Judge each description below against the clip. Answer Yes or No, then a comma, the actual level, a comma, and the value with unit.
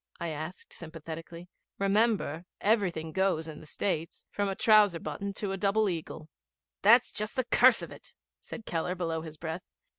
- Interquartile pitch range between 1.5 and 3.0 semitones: No, average, 4.0 semitones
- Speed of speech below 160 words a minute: No, average, 170 wpm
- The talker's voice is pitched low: No, medium, 180 Hz